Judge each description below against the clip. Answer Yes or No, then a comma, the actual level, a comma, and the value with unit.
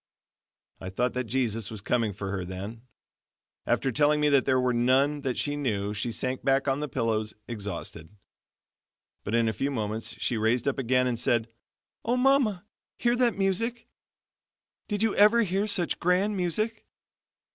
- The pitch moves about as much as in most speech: No, wide, 8.3 semitones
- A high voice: No, low, 130 Hz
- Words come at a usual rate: Yes, average, 170 wpm